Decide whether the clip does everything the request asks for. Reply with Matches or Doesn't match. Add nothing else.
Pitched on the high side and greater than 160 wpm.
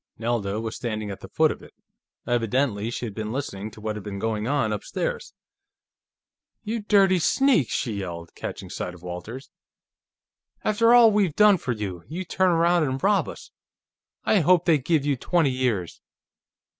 Doesn't match